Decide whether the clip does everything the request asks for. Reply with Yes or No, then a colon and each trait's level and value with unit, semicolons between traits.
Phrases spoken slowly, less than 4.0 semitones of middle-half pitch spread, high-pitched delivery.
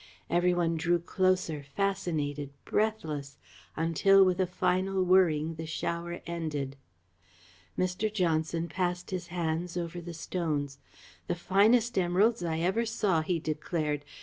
No: slow, 125 wpm; average, 2.7 semitones; medium, 175 Hz